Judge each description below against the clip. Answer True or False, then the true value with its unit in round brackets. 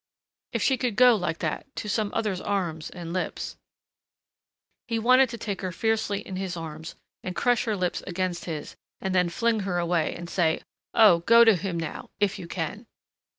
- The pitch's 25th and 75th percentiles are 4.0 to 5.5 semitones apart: True (4.4 semitones)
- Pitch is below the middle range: False (190 Hz)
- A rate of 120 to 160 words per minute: False (190 wpm)